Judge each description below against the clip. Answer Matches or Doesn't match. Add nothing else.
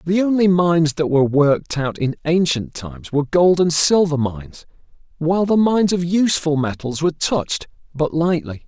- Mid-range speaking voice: Matches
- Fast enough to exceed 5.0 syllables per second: Matches